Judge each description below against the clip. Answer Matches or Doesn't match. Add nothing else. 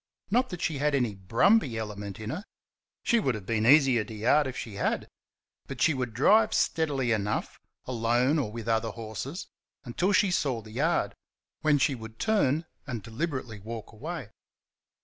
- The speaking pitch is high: Doesn't match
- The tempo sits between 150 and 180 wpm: Matches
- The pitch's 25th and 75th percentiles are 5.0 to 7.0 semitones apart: Matches